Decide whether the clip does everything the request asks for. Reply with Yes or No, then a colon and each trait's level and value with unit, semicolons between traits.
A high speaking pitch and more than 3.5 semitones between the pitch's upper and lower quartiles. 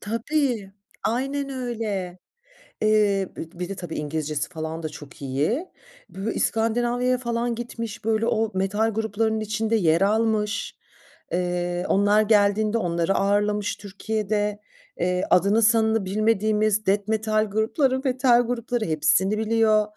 No: high, 215 Hz; average, 2.8 semitones